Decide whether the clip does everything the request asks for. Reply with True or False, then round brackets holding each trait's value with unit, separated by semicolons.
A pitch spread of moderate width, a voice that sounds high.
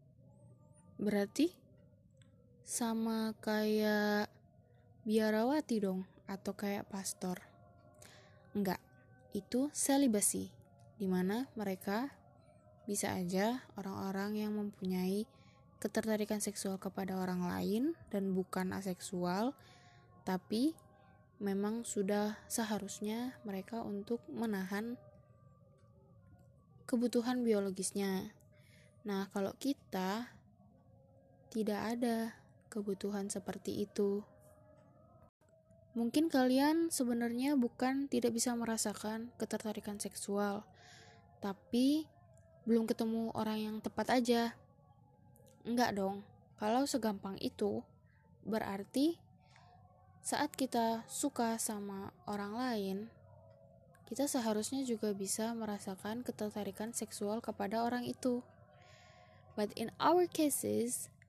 True (3.2 semitones; 210 Hz)